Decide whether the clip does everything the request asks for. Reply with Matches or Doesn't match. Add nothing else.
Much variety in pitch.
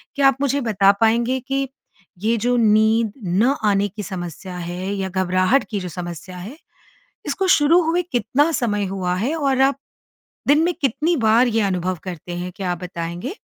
Matches